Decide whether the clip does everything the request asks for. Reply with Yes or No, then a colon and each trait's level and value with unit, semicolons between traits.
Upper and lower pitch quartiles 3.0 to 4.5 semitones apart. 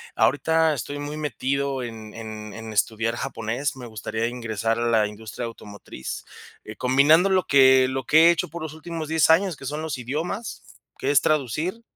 No: wide, 5.5 semitones